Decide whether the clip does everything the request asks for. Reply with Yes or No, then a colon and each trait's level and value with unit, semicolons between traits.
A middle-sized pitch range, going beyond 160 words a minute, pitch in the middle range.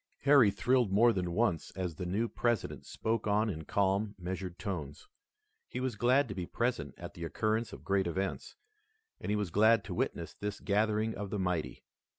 No: average, 3.5 semitones; average, 185 wpm; low, 100 Hz